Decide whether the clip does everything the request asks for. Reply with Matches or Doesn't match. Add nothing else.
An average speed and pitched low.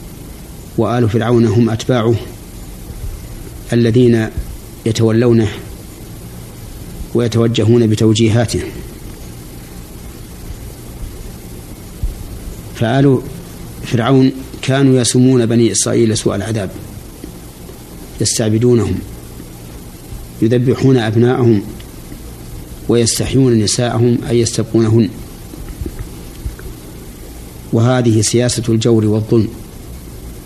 Doesn't match